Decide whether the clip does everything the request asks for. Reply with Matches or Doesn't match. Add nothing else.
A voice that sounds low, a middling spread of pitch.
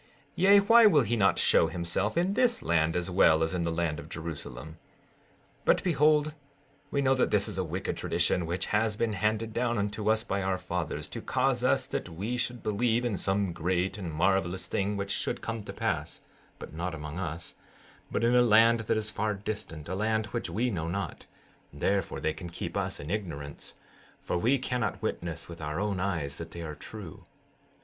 Matches